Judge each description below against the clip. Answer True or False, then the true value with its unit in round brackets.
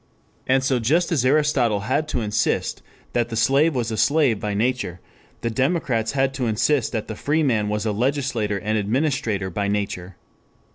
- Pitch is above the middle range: False (120 Hz)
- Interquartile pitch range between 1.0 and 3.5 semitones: False (4.4 semitones)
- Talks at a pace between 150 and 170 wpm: False (180 wpm)